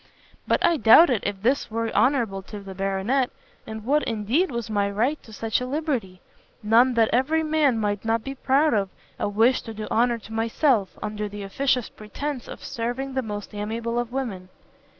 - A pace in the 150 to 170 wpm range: No, average, 190 wpm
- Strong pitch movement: No, average, 4.0 semitones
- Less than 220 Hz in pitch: No, high, 230 Hz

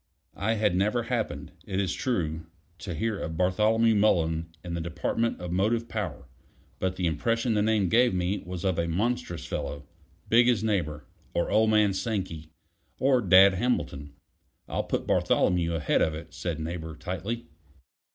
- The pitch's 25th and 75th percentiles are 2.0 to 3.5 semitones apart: No, average, 4.8 semitones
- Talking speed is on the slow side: No, average, 160 wpm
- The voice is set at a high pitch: No, very low, 95 Hz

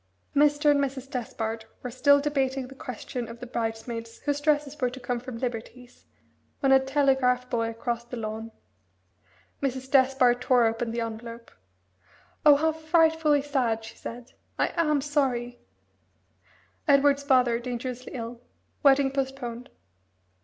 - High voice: Yes, very high, 255 Hz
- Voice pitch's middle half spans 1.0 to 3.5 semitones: Yes, average, 2.9 semitones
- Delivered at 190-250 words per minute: No, average, 140 wpm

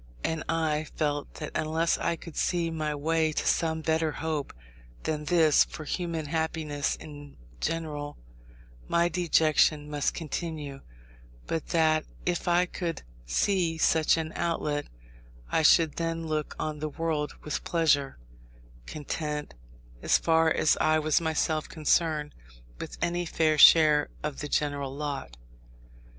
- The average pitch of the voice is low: No, medium, 155 Hz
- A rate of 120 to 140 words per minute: Yes, slow, 135 wpm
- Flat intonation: Yes, narrow, 1.7 semitones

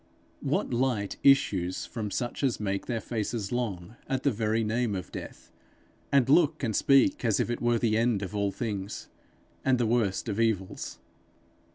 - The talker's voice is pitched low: Yes, low, 115 Hz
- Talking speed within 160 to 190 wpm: Yes, average, 175 wpm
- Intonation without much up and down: No, average, 3.3 semitones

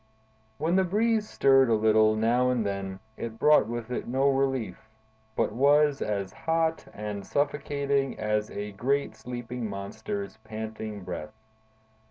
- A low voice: Yes, low, 120 Hz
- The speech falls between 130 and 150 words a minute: Yes, average, 140 wpm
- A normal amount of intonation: Yes, average, 4.7 semitones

